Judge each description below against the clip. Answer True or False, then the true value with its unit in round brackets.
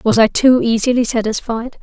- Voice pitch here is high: True (235 Hz)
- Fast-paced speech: False (165 wpm)